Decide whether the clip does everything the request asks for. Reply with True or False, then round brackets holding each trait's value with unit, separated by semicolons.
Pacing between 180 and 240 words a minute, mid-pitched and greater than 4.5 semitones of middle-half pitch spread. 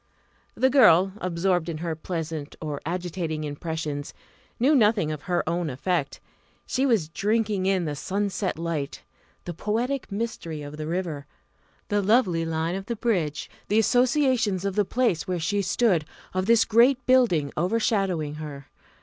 False (150 wpm; 180 Hz; 5.4 semitones)